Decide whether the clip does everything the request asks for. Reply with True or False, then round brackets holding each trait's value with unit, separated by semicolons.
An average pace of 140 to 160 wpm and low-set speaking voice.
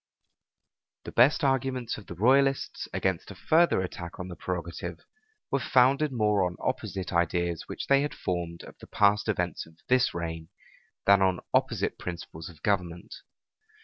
True (155 wpm; 95 Hz)